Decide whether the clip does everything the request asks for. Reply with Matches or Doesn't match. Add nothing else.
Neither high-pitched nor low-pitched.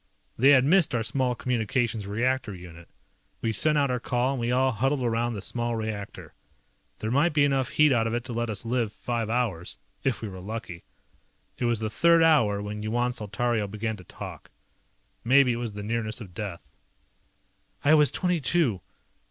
Doesn't match